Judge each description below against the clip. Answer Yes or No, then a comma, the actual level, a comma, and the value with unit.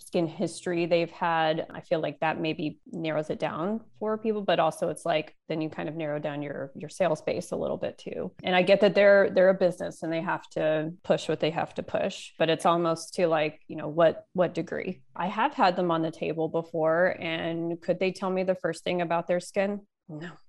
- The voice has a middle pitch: Yes, medium, 170 Hz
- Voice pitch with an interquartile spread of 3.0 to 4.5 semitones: No, narrow, 2.6 semitones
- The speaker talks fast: Yes, fast, 235 wpm